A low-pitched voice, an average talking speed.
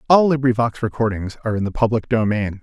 Yes: low, 115 Hz; average, 185 wpm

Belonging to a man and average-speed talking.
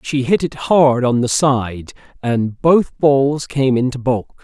Yes: male; average, 175 wpm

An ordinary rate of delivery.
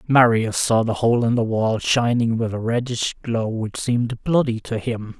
Yes: average, 195 wpm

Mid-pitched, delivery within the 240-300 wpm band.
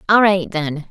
No: medium, 180 Hz; average, 200 wpm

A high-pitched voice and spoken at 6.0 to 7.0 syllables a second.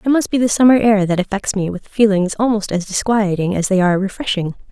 Yes: high, 205 Hz; 6.1 syllables/s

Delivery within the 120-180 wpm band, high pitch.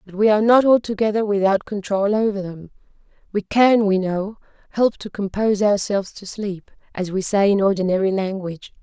Yes: average, 170 wpm; high, 200 Hz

